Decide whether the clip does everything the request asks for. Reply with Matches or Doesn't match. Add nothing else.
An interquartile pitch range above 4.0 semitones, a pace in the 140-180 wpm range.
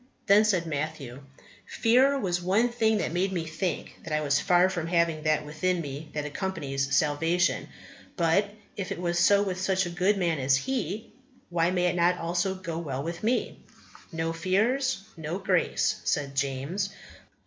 Doesn't match